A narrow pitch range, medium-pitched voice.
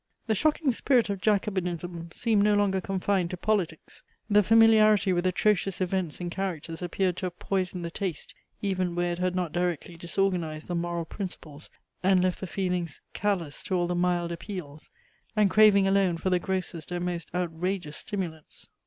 Yes: narrow, 2.3 semitones; medium, 180 Hz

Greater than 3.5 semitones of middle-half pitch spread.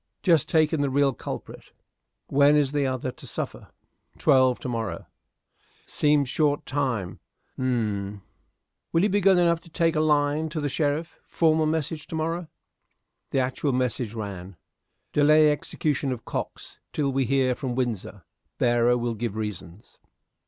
Yes: average, 4.3 semitones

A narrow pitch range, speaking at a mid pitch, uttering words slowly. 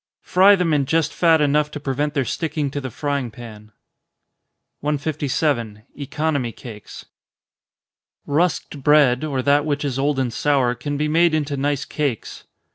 No: narrow, 2.3 semitones; medium, 145 Hz; average, 150 wpm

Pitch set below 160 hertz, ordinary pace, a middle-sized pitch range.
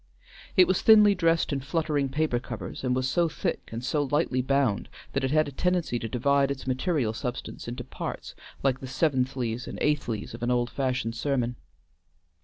Yes: low, 135 Hz; average, 185 wpm; average, 3.5 semitones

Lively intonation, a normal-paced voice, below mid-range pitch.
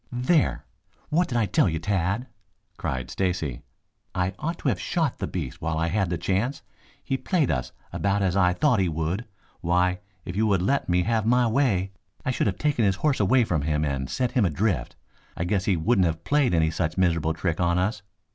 No: wide, 6.1 semitones; fast, 210 wpm; very low, 95 Hz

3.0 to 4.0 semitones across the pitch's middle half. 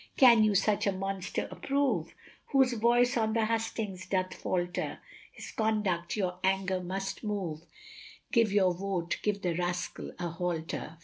Yes: average, 3.5 semitones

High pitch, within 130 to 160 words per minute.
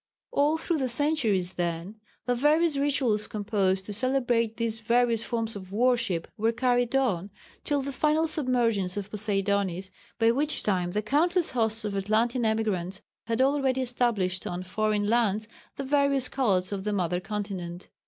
Yes: high, 225 Hz; average, 155 wpm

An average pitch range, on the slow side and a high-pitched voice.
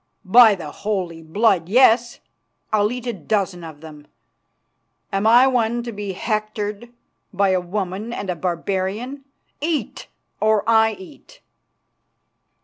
Yes: average, 4.1 semitones; slow, 130 wpm; high, 210 Hz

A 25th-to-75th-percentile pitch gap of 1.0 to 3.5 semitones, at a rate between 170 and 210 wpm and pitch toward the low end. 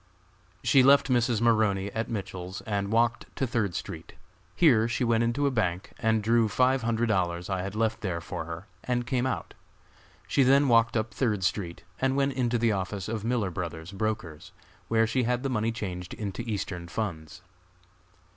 No: average, 4.0 semitones; average, 180 wpm; low, 110 Hz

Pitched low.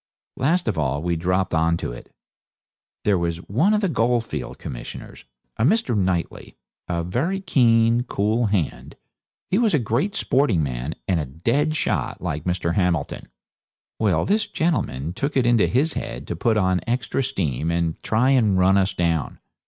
Yes: low, 100 Hz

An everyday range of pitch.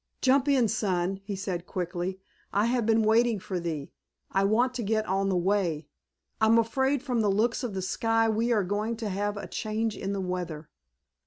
Yes: average, 3.3 semitones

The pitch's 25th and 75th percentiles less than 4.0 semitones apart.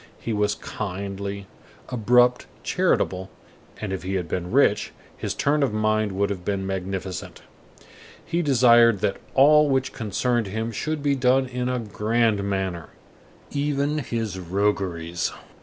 No: average, 4.5 semitones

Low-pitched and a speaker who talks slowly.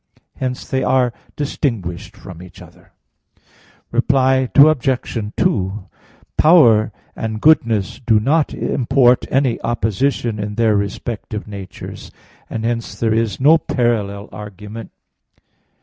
Yes: low, 115 Hz; slow, 110 wpm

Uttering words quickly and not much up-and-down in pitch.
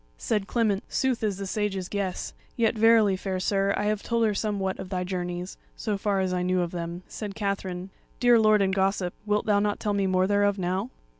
Yes: fast, 215 wpm; narrow, 2.1 semitones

